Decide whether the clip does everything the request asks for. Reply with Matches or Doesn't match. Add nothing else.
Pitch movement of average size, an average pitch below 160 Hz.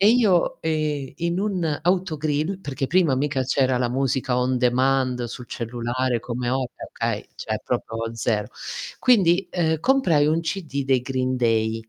Matches